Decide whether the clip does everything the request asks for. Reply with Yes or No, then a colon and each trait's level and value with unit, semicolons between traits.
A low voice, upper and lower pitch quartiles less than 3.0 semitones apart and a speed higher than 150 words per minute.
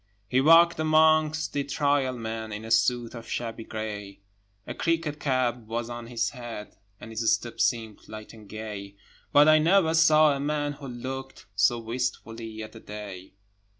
No: low, 120 Hz; average, 4.8 semitones; average, 170 wpm